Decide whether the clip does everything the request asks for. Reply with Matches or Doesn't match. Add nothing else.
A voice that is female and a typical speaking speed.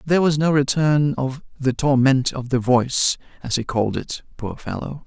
Doesn't match